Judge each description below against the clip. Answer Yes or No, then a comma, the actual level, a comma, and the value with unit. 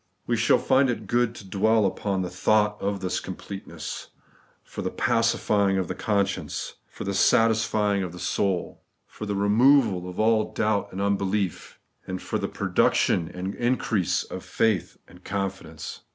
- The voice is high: No, low, 100 Hz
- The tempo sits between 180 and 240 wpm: No, average, 165 wpm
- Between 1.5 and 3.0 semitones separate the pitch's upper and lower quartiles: Yes, average, 2.7 semitones